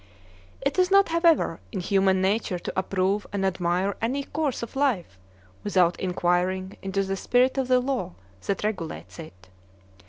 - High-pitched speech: Yes, high, 195 Hz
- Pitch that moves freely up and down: Yes, wide, 5.8 semitones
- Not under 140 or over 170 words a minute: Yes, average, 155 wpm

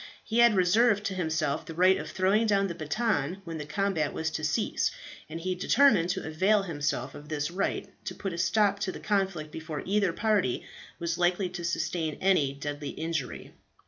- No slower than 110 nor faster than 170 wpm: No, average, 190 wpm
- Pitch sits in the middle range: Yes, medium, 175 Hz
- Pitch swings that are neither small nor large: Yes, average, 4.0 semitones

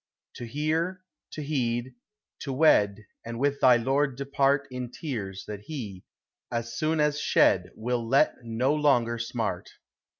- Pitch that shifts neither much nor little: Yes, average, 3.9 semitones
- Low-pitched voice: Yes, low, 125 Hz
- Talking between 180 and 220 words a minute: No, average, 140 wpm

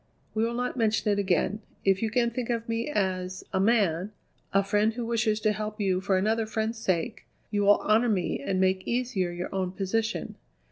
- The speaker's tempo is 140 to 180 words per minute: No, average, 200 wpm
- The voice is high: Yes, high, 210 Hz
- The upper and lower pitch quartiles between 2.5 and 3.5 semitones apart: Yes, average, 3.2 semitones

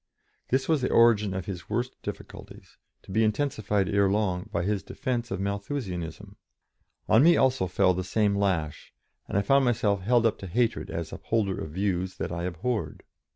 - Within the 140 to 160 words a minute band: No, average, 180 wpm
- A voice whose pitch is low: Yes, low, 100 Hz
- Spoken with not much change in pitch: No, average, 4.1 semitones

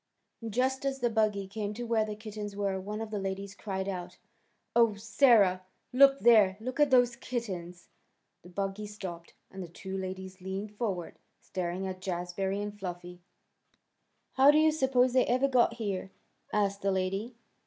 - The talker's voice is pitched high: Yes, high, 205 Hz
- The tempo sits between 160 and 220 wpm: Yes, average, 165 wpm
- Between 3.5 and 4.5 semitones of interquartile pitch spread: Yes, average, 3.8 semitones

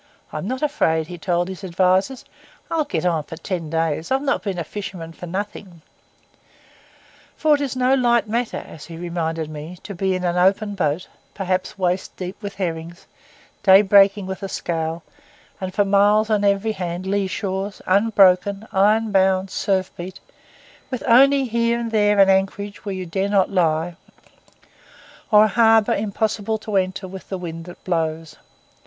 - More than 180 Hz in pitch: Yes, high, 190 Hz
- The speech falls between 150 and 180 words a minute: Yes, average, 175 wpm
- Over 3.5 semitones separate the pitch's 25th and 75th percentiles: No, average, 3.1 semitones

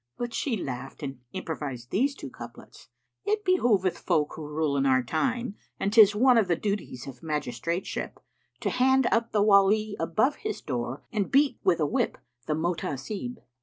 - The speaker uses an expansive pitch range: Yes, wide, 8.0 semitones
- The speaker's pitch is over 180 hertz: Yes, high, 190 Hz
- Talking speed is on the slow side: No, average, 180 wpm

